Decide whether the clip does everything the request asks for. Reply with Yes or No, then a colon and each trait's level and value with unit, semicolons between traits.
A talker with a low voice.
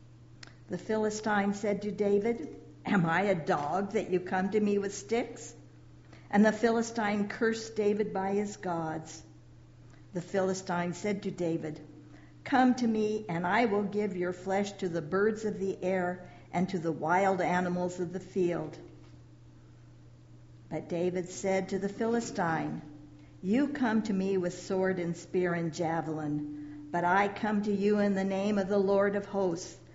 No: high, 190 Hz